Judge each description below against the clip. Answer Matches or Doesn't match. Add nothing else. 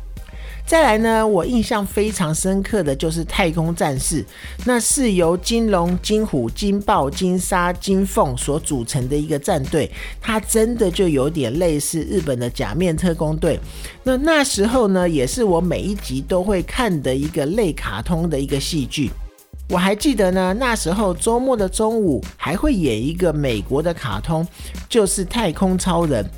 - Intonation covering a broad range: Matches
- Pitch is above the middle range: Doesn't match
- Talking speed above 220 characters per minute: Matches